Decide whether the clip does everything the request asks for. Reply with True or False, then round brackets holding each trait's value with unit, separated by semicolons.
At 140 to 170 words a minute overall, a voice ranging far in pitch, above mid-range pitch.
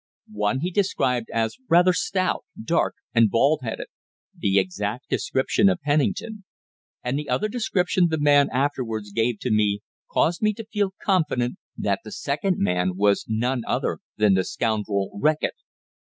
False (150 wpm; 8.7 semitones; 130 Hz)